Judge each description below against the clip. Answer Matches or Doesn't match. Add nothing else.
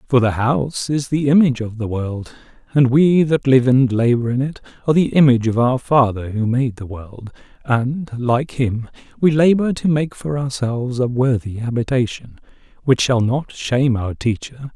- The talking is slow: Doesn't match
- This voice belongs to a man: Matches